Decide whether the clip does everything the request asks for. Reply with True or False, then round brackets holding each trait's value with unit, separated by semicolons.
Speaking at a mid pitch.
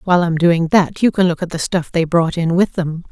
True (170 Hz)